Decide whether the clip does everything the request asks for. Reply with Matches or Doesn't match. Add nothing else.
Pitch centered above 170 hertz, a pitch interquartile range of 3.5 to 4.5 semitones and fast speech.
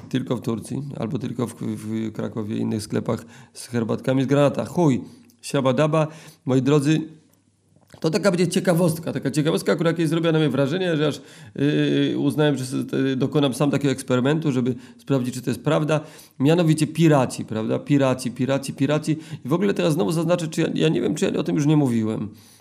Doesn't match